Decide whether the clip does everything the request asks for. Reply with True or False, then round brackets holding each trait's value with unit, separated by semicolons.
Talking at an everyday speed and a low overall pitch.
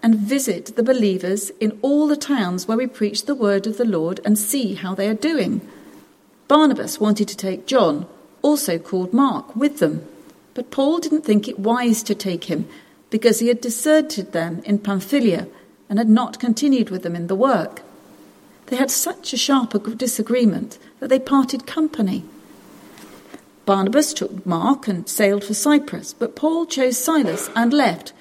False (170 wpm; 230 Hz)